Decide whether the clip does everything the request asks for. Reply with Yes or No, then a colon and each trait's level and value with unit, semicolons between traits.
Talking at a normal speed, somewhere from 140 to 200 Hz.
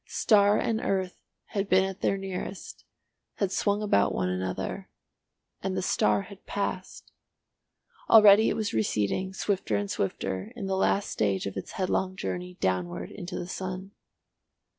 Yes: average, 150 wpm; medium, 185 Hz